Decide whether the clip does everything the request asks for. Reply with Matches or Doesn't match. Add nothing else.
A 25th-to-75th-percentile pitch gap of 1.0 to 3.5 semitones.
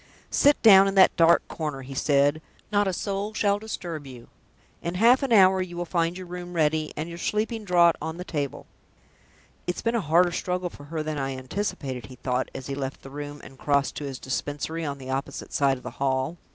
Doesn't match